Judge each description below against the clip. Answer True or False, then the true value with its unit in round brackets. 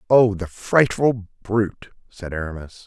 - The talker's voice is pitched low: True (105 Hz)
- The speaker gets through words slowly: True (125 wpm)